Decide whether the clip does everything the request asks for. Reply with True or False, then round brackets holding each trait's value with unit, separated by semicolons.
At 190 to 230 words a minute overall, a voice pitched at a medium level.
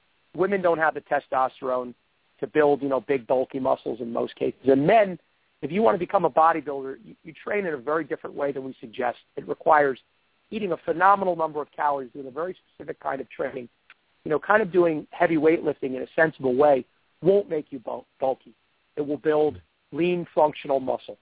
True (200 wpm; 150 Hz)